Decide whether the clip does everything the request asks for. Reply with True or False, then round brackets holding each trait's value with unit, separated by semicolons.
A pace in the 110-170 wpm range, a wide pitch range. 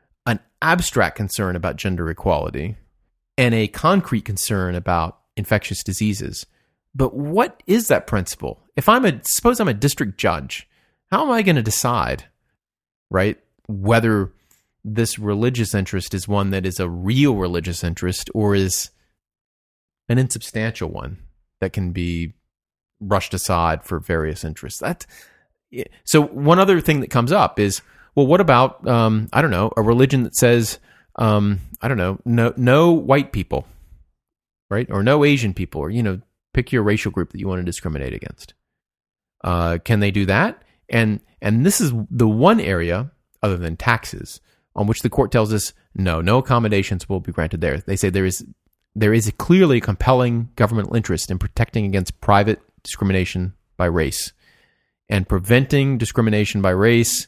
False (165 wpm; 4.5 semitones)